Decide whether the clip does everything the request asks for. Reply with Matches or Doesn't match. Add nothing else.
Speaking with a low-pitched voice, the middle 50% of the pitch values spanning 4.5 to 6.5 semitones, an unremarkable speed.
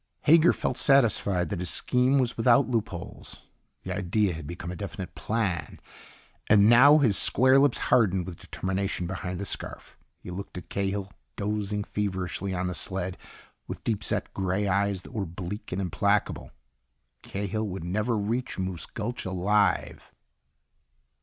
Doesn't match